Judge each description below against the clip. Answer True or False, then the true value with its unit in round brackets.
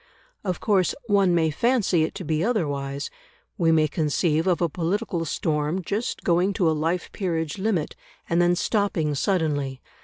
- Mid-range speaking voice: True (170 Hz)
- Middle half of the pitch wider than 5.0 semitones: False (3.6 semitones)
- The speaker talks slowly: False (160 wpm)